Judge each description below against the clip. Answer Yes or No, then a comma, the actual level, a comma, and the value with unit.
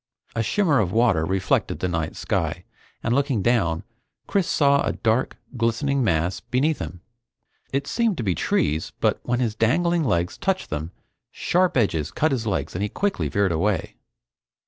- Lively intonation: Yes, wide, 7.7 semitones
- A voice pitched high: No, low, 115 Hz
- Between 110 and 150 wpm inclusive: No, average, 170 wpm